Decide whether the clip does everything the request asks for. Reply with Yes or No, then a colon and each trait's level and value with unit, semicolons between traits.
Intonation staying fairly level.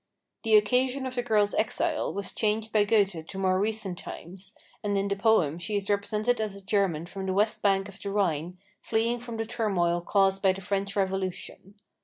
Yes: narrow, 2.3 semitones